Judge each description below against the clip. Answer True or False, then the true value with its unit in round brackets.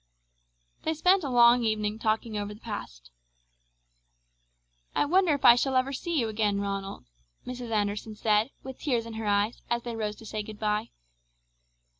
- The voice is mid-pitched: False (225 Hz)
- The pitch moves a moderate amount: True (3.1 semitones)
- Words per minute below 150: False (165 wpm)